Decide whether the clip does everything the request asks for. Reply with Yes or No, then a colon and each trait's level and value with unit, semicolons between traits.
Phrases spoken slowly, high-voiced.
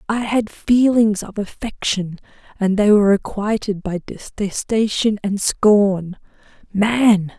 Yes: slow, 115 wpm; high, 205 Hz